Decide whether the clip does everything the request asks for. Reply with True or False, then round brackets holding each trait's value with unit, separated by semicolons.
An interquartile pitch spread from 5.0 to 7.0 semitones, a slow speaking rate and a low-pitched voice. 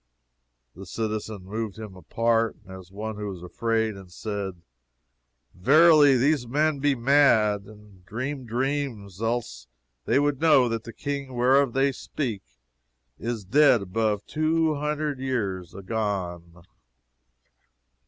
True (5.6 semitones; 125 wpm; 115 Hz)